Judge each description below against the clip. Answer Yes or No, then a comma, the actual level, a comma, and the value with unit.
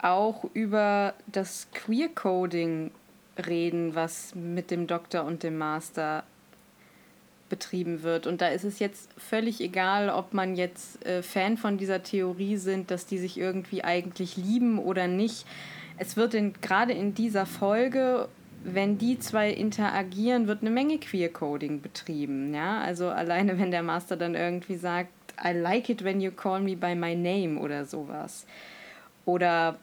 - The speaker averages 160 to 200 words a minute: No, average, 150 wpm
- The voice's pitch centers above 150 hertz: Yes, medium, 185 Hz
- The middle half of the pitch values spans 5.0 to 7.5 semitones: No, average, 3.1 semitones